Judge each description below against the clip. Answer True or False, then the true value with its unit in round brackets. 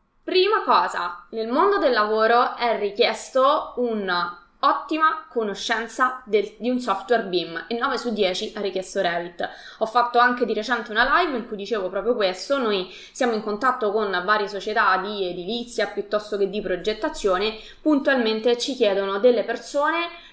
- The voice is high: True (225 Hz)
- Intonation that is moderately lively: True (3.7 semitones)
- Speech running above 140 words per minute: True (155 wpm)